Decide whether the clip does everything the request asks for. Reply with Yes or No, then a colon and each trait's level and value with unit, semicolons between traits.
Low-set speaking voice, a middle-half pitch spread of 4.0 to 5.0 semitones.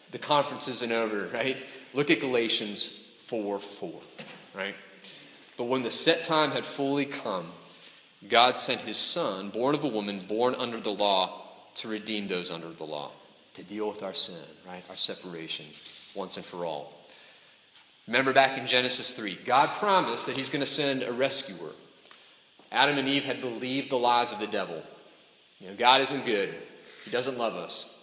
Yes: low, 125 Hz; average, 4.5 semitones